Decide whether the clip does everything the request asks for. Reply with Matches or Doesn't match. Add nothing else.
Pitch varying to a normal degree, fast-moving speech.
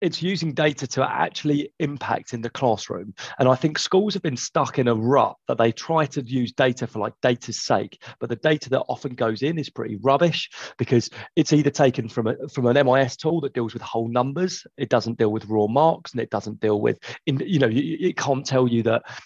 Matches